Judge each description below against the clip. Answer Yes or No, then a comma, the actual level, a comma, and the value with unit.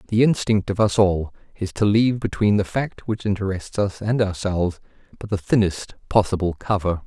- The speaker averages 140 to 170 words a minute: No, average, 180 wpm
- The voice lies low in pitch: Yes, low, 100 Hz